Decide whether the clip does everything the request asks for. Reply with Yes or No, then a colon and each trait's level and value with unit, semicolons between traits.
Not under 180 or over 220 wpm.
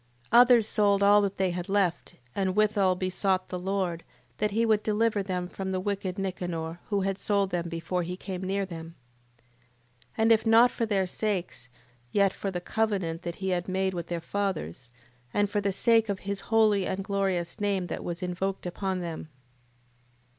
Yes: average, 190 wpm